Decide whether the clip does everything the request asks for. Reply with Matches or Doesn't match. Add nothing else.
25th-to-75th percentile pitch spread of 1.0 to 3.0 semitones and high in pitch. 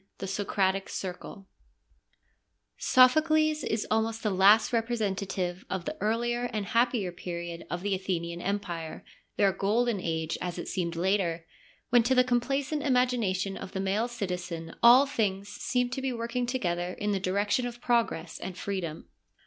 Doesn't match